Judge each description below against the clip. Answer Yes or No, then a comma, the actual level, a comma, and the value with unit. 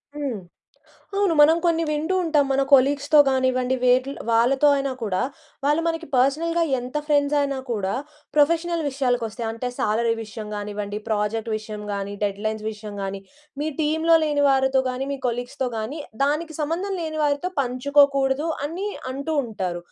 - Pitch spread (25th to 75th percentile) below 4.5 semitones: No, average, 5.0 semitones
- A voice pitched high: Yes, very high, 270 Hz